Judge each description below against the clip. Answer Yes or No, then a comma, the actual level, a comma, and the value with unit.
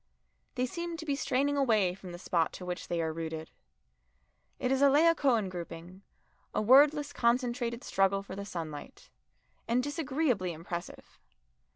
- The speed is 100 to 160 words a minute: Yes, average, 150 wpm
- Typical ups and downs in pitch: No, wide, 7.8 semitones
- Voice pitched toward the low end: No, high, 230 Hz